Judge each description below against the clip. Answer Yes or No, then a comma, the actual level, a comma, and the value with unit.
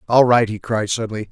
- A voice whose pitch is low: Yes, low, 110 Hz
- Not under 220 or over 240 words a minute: Yes, fast, 230 wpm